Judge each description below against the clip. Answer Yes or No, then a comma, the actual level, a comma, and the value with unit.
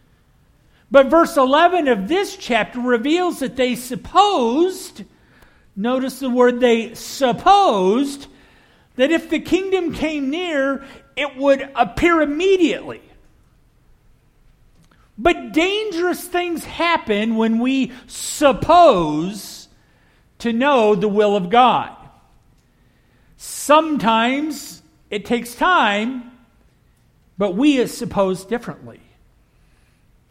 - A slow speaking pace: Yes, slow, 95 wpm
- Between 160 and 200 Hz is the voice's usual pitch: No, very high, 265 Hz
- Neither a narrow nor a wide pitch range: No, wide, 5.8 semitones